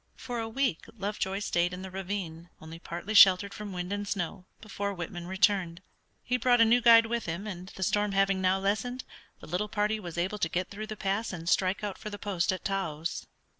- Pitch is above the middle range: Yes, high, 195 Hz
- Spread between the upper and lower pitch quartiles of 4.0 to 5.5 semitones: No, average, 2.9 semitones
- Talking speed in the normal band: No, fast, 215 wpm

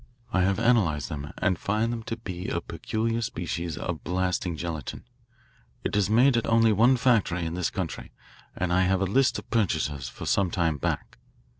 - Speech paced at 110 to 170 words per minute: No, average, 185 wpm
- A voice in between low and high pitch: No, very low, 95 Hz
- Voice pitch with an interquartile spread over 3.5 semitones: Yes, average, 5.0 semitones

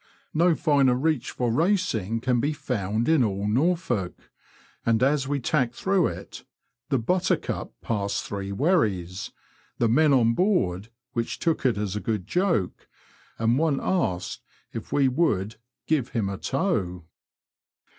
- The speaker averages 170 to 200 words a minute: No, average, 145 wpm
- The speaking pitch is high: No, low, 125 Hz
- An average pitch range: No, wide, 7.0 semitones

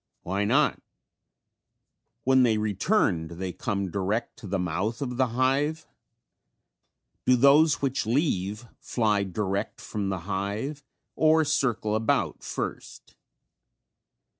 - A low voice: Yes, low, 110 Hz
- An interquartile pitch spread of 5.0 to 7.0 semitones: Yes, wide, 5.4 semitones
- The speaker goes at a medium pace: No, slow, 115 wpm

